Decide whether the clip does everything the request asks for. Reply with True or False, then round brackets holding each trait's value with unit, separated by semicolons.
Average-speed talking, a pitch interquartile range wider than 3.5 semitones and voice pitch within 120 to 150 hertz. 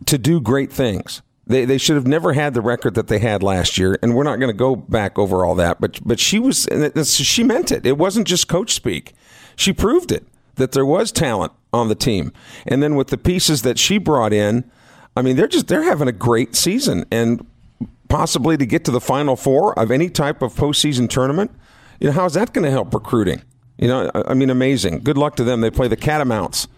False (240 wpm; 3.9 semitones; 135 Hz)